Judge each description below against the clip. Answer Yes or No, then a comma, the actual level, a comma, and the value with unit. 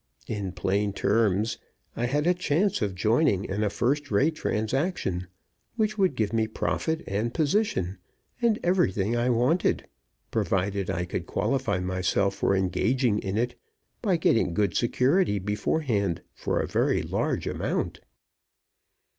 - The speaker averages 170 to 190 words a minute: No, average, 140 wpm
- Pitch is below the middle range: Yes, low, 110 Hz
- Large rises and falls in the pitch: Yes, wide, 7.0 semitones